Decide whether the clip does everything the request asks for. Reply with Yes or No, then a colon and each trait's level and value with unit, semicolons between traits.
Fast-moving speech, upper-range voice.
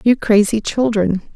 No: slow, 135 wpm; high, 215 Hz